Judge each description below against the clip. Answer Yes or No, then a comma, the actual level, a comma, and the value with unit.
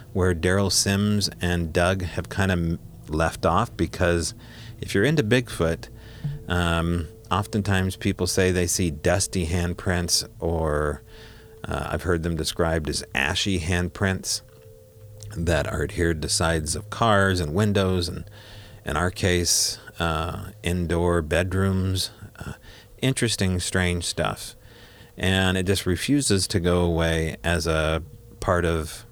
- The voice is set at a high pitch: No, very low, 95 Hz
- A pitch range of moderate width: Yes, average, 3.6 semitones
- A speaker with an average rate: No, slow, 130 wpm